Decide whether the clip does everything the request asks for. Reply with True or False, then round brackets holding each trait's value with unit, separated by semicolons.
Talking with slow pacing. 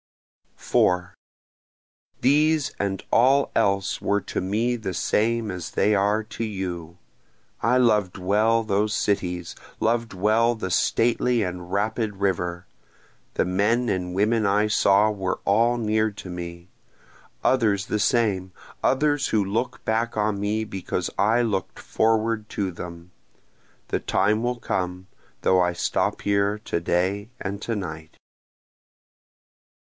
True (130 wpm)